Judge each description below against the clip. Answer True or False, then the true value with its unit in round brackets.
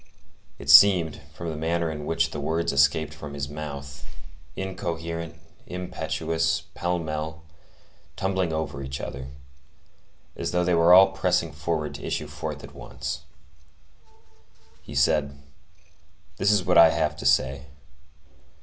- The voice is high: False (80 Hz)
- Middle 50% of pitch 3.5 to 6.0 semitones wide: False (2.9 semitones)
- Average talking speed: False (130 wpm)